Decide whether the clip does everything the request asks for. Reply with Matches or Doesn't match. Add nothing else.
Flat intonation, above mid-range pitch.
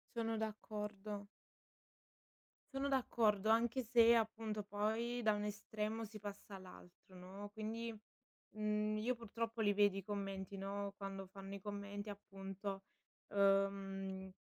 Matches